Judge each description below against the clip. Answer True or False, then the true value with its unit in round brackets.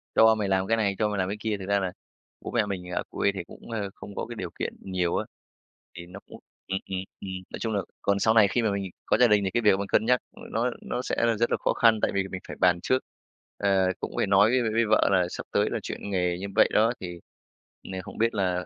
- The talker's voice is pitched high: False (100 Hz)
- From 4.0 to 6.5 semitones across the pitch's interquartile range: False (2.8 semitones)